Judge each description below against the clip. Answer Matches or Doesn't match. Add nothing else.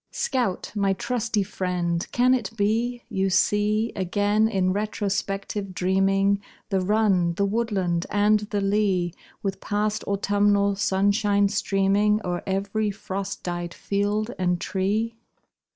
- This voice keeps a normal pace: Doesn't match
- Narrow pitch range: Matches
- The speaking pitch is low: Doesn't match